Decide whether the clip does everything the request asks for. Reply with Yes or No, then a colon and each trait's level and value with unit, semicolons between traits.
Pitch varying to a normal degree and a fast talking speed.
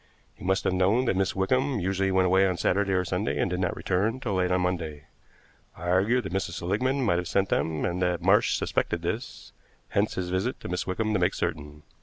No: narrow, 2.3 semitones; fast, 225 wpm